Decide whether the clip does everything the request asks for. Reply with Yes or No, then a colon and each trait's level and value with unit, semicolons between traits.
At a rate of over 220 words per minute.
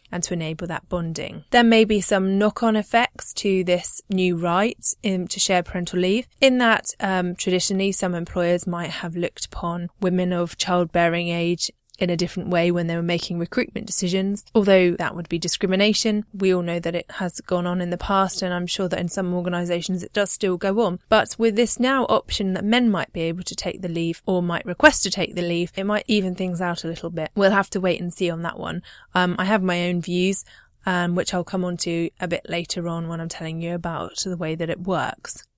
Yes: fast, 230 wpm